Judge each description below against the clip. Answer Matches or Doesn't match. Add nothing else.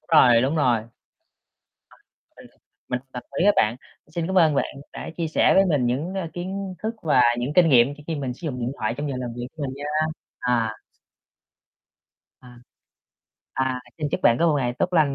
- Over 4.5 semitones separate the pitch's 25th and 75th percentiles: Matches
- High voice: Doesn't match